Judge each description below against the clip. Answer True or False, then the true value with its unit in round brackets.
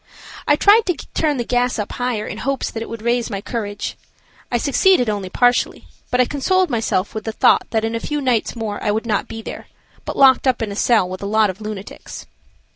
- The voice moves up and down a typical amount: True (3.2 semitones)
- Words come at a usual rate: False (230 wpm)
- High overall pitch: True (230 Hz)